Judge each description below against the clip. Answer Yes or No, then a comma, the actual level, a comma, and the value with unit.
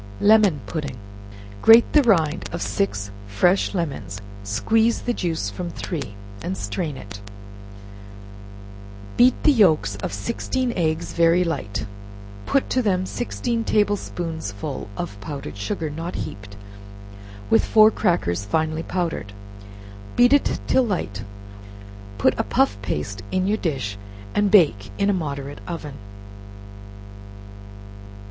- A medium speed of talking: No, slow, 125 wpm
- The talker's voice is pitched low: No, medium, 160 Hz